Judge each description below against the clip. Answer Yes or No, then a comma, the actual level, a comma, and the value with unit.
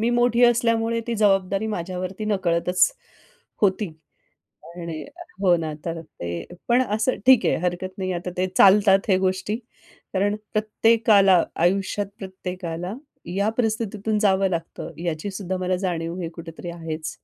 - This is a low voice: No, high, 190 Hz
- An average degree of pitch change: Yes, average, 3.3 semitones